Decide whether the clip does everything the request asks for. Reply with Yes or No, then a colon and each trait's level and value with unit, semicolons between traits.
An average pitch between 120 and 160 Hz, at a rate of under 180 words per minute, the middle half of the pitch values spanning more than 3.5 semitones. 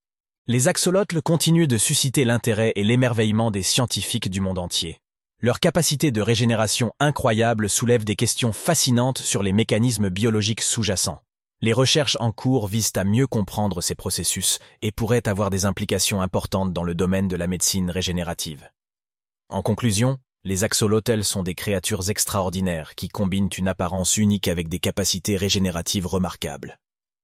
No: low, 105 Hz; average, 150 wpm; average, 4.0 semitones